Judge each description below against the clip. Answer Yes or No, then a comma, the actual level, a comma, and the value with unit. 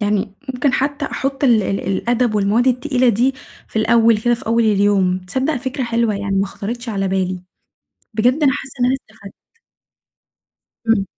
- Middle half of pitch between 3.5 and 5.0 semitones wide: Yes, average, 4.1 semitones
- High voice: Yes, high, 230 Hz